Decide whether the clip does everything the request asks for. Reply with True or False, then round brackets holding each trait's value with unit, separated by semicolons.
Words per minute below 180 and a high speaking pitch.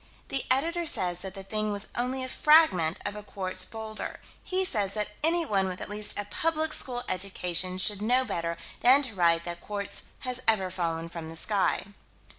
False (190 wpm; 205 Hz)